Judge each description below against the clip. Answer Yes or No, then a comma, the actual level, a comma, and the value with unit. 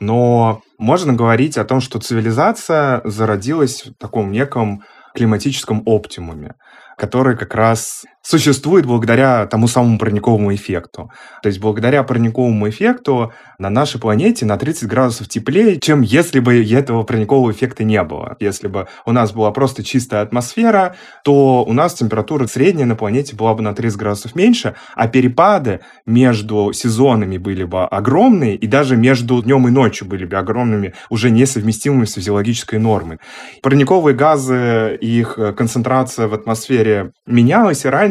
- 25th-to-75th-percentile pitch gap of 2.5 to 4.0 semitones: Yes, average, 3.5 semitones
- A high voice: No, low, 115 Hz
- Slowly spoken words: No, average, 145 wpm